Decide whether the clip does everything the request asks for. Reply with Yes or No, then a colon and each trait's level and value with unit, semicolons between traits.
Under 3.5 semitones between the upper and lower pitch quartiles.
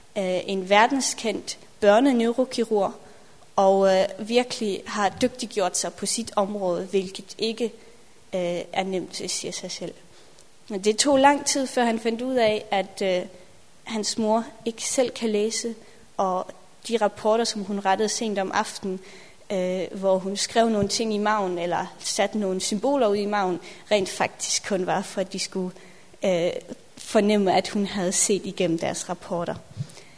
Yes: average, 2.9 semitones